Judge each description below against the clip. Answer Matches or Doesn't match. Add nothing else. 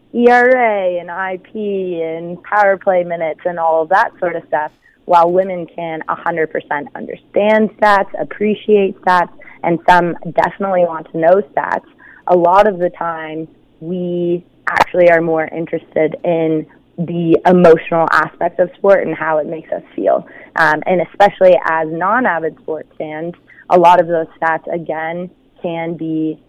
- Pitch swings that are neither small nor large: Doesn't match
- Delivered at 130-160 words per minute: Matches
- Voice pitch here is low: Doesn't match